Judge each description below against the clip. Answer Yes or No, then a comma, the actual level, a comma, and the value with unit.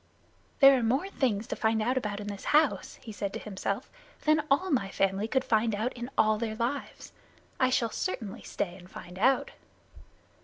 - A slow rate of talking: No, average, 190 wpm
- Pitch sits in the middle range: No, high, 225 Hz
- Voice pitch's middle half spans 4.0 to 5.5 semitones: Yes, average, 4.4 semitones